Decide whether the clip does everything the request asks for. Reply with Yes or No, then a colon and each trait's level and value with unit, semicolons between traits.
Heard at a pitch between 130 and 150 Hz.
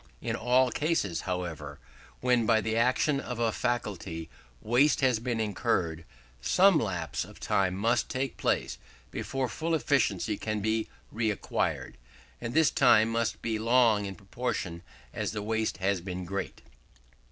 No: low, 110 Hz